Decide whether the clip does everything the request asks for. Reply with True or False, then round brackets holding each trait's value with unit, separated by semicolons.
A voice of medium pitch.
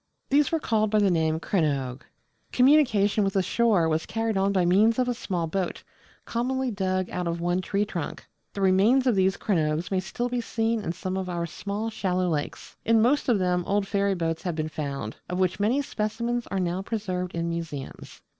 False (195 Hz)